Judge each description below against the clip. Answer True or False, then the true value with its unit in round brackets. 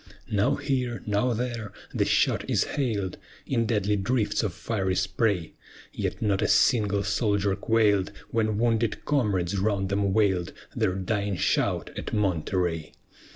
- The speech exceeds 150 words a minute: False (140 wpm)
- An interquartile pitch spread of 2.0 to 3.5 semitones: True (2.9 semitones)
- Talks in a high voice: False (105 Hz)